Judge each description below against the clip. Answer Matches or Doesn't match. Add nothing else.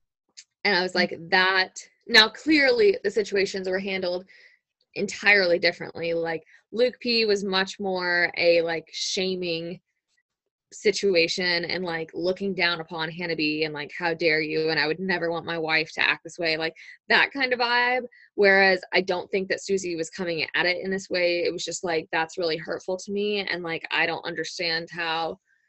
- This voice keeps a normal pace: Matches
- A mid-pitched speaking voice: Matches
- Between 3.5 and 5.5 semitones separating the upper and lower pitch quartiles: Doesn't match